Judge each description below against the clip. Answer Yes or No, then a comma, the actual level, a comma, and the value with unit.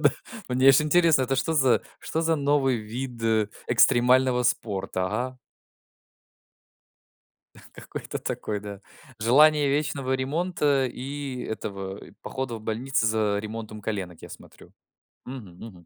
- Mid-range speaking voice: No, low, 125 Hz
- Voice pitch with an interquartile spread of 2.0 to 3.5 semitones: No, average, 4.2 semitones